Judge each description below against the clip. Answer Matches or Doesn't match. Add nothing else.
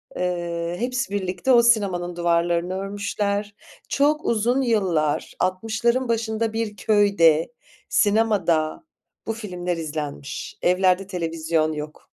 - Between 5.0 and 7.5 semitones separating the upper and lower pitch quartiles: Doesn't match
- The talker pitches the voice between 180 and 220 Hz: Matches